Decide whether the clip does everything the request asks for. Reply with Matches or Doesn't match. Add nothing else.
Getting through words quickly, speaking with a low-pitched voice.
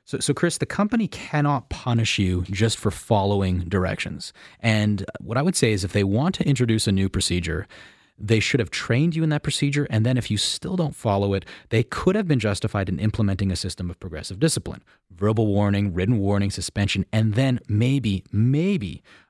Doesn't match